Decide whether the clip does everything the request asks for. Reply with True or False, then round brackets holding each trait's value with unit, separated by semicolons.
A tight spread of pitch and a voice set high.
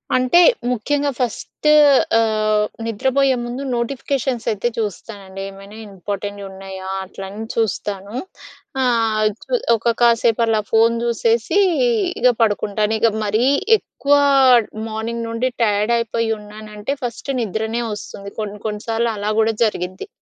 True (2.2 semitones; 220 Hz)